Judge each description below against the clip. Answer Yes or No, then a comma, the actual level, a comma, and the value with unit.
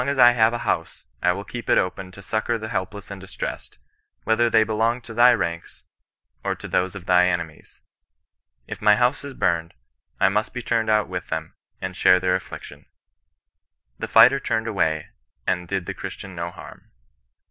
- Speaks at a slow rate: No, average, 190 wpm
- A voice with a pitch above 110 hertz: No, low, 100 Hz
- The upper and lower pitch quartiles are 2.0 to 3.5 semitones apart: No, average, 4.1 semitones